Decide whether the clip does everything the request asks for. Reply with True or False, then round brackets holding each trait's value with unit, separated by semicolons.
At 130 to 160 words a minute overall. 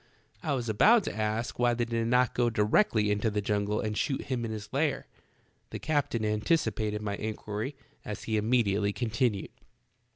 False (175 wpm)